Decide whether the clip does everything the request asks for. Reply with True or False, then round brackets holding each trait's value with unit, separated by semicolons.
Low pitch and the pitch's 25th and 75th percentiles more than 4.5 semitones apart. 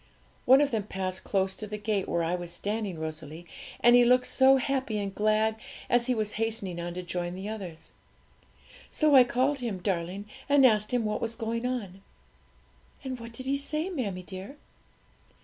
False (215 Hz; 4.9 semitones)